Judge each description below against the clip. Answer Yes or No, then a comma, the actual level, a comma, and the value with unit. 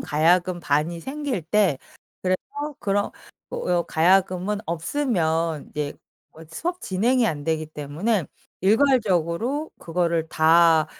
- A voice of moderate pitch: Yes, medium, 175 Hz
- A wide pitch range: No, average, 4.7 semitones